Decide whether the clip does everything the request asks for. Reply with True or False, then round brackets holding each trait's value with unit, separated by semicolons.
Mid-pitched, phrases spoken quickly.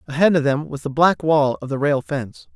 True (145 Hz; 260 wpm)